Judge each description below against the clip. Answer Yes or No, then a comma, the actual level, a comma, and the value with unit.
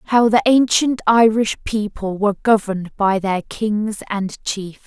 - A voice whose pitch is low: No, high, 210 Hz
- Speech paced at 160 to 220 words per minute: No, average, 150 wpm